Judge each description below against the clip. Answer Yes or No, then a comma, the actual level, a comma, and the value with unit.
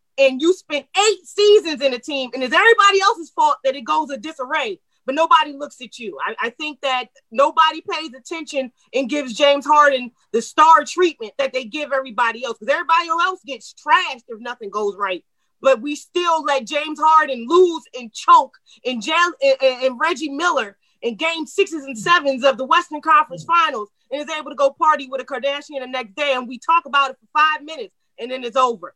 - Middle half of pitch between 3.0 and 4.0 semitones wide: Yes, average, 3.7 semitones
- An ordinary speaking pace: No, fast, 210 wpm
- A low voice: No, very high, 285 Hz